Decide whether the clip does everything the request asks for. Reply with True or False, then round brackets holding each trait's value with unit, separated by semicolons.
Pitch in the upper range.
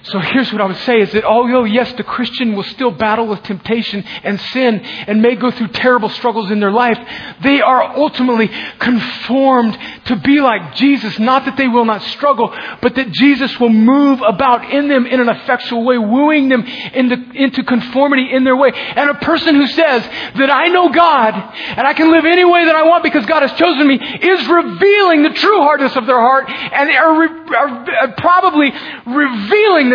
True (255 Hz)